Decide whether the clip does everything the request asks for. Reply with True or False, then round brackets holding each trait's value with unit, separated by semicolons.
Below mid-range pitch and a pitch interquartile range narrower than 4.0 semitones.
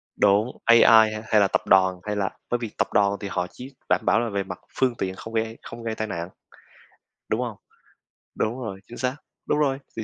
True (110 Hz; 3.0 semitones)